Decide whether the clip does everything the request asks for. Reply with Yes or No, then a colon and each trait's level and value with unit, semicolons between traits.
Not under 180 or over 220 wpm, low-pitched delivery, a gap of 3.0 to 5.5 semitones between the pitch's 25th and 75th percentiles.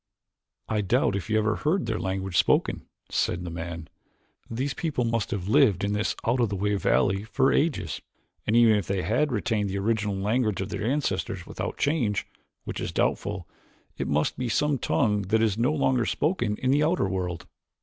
Yes: average, 190 wpm; low, 110 Hz; average, 4.5 semitones